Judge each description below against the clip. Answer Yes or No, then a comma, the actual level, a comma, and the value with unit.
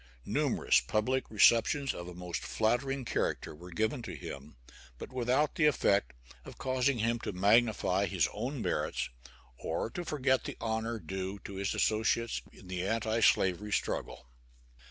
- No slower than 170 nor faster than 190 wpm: No, average, 155 wpm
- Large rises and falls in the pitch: No, average, 4.6 semitones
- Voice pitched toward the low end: Yes, low, 110 Hz